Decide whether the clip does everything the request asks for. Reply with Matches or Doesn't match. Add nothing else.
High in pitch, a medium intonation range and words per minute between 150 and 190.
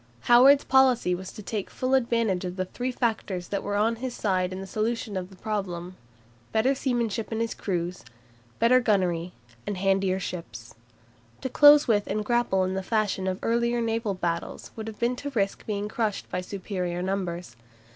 Matches